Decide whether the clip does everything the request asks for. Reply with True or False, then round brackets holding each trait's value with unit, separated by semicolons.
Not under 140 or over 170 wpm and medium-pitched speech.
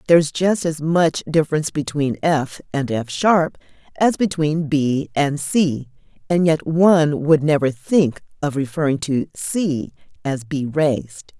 True (145 wpm; 150 Hz)